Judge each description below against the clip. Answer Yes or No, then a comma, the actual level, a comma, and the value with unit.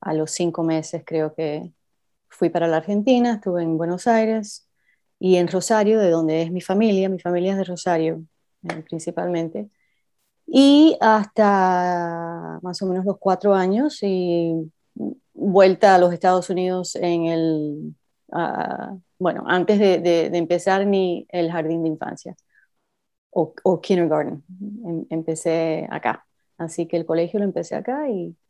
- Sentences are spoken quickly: No, average, 145 wpm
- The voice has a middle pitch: Yes, medium, 175 Hz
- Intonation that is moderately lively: Yes, average, 3.1 semitones